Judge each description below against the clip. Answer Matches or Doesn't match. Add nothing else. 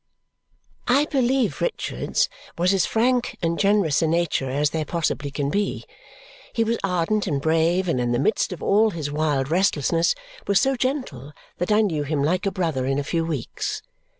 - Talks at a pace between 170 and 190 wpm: Matches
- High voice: Doesn't match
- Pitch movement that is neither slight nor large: Doesn't match